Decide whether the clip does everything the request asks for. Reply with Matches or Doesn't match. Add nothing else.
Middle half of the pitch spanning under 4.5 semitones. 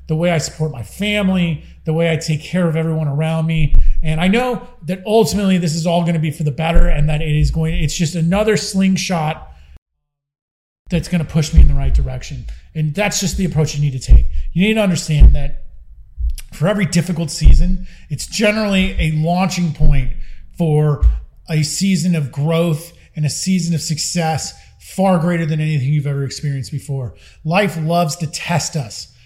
Matches